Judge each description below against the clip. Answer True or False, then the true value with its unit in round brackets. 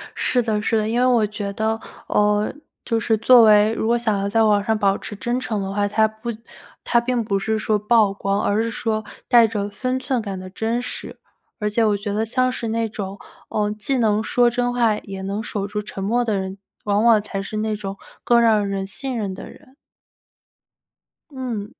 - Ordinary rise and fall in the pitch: False (2.3 semitones)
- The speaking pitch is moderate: False (215 Hz)